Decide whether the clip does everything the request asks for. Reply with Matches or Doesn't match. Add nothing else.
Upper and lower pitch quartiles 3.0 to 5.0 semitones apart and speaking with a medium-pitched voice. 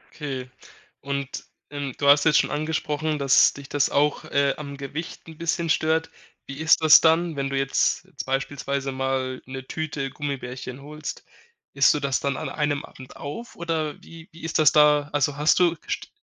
Doesn't match